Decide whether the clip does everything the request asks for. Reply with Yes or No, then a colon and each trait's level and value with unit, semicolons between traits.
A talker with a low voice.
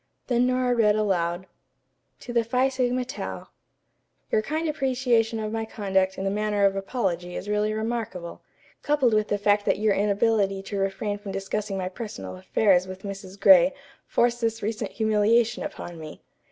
No: high, 210 Hz